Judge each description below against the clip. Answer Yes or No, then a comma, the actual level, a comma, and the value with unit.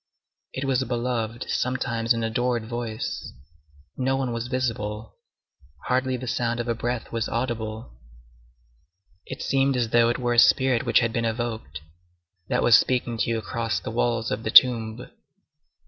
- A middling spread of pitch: No, narrow, 1.8 semitones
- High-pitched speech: No, low, 120 Hz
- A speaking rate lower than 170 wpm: Yes, average, 160 wpm